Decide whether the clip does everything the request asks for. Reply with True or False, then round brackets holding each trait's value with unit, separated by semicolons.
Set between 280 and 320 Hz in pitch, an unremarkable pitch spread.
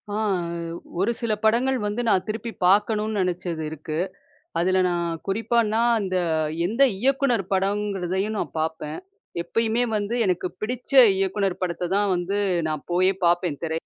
False (195 Hz; 3.8 semitones)